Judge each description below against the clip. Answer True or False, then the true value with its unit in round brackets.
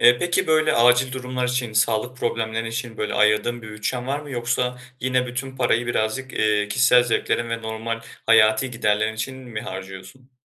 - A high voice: False (120 Hz)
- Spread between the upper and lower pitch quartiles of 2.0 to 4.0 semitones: True (2.5 semitones)